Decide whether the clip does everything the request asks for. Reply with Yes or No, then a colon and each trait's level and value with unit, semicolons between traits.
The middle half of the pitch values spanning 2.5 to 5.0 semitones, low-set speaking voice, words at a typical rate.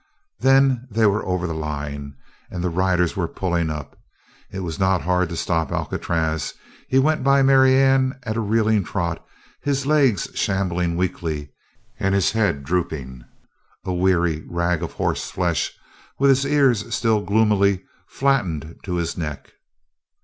No: wide, 5.6 semitones; very low, 95 Hz; average, 145 wpm